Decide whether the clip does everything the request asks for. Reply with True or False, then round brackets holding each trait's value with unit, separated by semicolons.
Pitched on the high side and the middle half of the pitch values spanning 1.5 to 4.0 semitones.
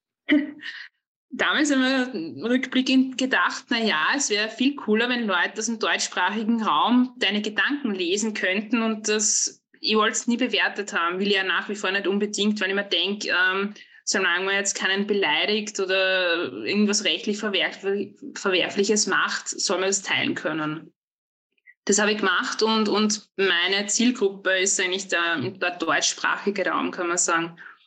True (210 Hz; 3.3 semitones)